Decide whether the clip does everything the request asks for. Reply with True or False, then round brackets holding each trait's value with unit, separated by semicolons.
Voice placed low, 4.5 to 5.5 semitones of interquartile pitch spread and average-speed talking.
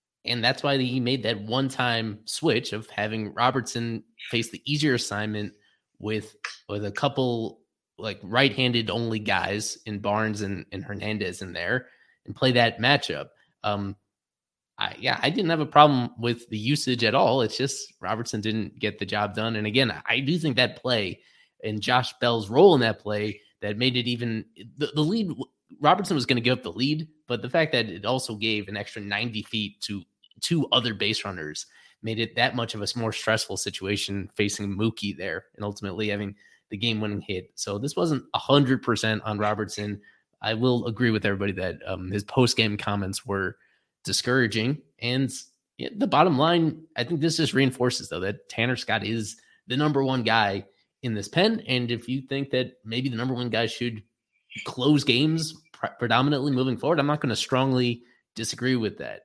False (115 Hz; 3.7 semitones; 190 wpm)